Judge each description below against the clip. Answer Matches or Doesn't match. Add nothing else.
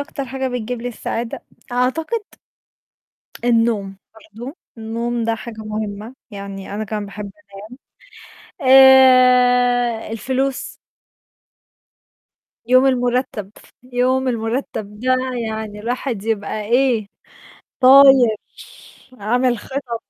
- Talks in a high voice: Matches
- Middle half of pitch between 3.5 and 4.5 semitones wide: Doesn't match